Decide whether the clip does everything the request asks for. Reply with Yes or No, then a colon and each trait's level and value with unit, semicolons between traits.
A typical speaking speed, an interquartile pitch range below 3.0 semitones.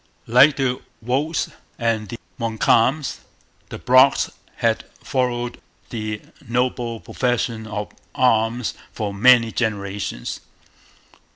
No: slow, 95 wpm; narrow, 2.4 semitones